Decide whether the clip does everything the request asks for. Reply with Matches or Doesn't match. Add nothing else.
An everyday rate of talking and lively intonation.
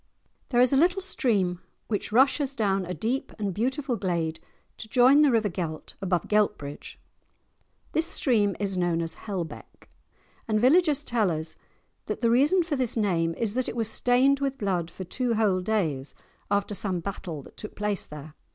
Matches